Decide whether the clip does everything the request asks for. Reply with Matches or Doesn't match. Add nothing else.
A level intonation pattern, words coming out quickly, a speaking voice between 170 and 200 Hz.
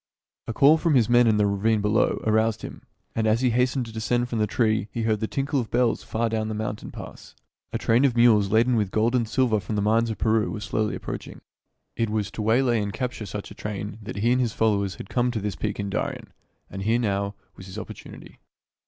Doesn't match